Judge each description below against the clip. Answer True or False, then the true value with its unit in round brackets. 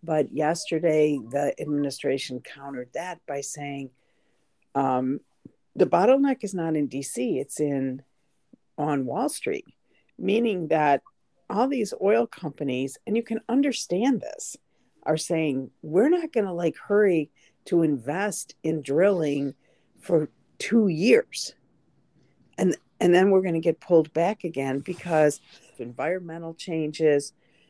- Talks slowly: True (125 wpm)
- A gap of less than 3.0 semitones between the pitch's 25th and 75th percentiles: False (5.6 semitones)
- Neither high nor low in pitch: True (160 Hz)